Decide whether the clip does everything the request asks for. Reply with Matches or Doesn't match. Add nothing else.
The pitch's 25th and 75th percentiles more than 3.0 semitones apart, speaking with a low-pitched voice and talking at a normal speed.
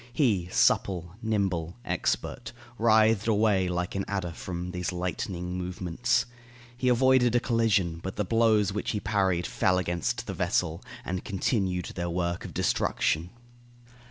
Matches